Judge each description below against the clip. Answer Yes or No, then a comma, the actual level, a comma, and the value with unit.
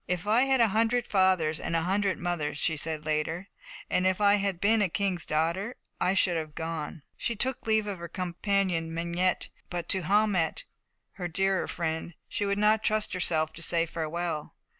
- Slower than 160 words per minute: No, average, 190 wpm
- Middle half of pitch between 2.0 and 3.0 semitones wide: No, average, 3.7 semitones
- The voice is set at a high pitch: No, medium, 180 Hz